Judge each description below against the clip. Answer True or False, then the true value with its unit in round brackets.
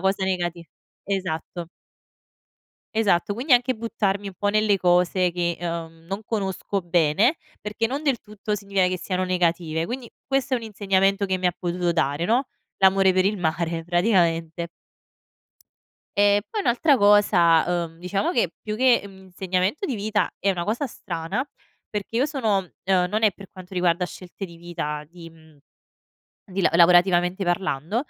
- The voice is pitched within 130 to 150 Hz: False (190 Hz)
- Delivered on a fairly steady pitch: False (3.3 semitones)